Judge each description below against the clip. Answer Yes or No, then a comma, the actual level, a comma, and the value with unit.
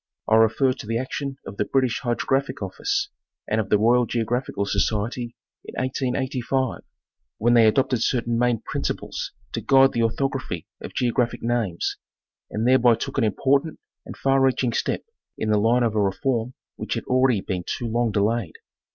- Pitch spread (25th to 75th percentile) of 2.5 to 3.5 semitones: Yes, average, 2.8 semitones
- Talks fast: No, average, 170 wpm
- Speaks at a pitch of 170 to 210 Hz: No, low, 120 Hz